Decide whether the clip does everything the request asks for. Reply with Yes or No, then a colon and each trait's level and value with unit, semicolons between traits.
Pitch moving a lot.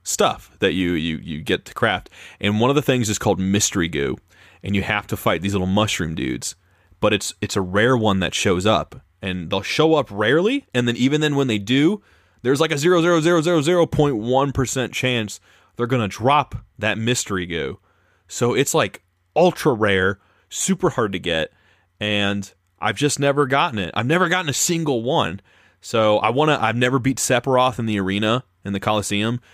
Yes: wide, 5.9 semitones